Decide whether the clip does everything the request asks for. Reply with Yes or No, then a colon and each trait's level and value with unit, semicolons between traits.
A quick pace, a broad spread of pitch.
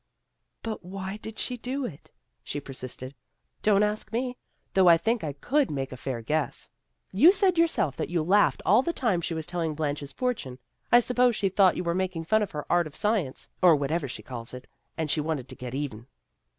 Yes: fast, 220 wpm; wide, 7.2 semitones